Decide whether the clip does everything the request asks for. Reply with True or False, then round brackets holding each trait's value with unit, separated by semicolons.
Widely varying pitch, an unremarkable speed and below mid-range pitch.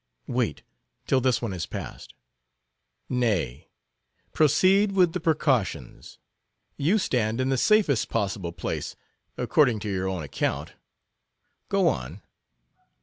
False (8.2 semitones; 115 wpm; 120 Hz)